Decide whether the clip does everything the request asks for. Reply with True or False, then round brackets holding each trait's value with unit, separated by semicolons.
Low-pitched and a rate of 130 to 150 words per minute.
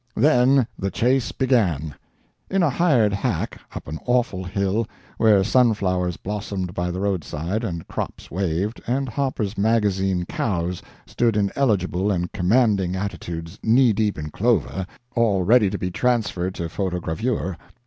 True (100 Hz; 140 wpm)